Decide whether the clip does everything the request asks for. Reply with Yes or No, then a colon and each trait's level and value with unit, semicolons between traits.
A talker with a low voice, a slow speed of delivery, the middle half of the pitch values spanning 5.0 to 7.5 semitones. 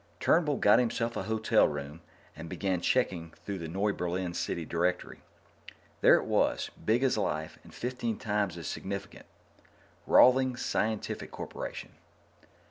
Yes: low, 100 Hz; slow, 130 wpm; average, 5.3 semitones